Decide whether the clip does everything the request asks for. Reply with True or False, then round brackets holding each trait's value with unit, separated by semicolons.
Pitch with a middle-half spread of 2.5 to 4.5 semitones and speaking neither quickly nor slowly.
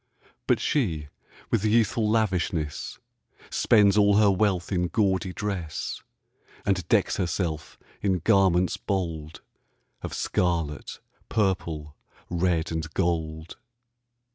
False (3.8 semitones; 100 wpm)